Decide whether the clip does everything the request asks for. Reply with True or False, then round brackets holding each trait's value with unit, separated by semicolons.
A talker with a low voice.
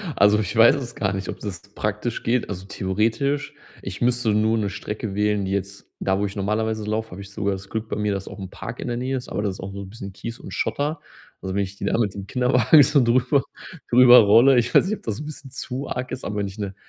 True (105 Hz)